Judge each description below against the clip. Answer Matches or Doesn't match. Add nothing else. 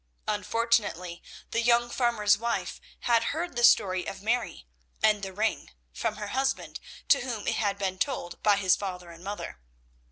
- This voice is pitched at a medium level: Doesn't match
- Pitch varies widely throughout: Doesn't match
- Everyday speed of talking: Matches